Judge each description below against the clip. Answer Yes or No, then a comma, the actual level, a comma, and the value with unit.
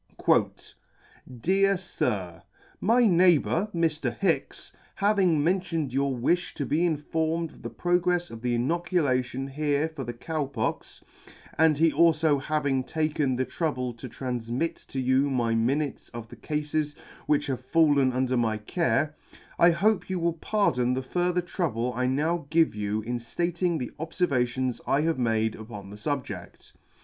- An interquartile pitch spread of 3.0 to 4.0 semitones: No, average, 5.1 semitones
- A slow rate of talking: No, average, 155 wpm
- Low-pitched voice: No, medium, 145 Hz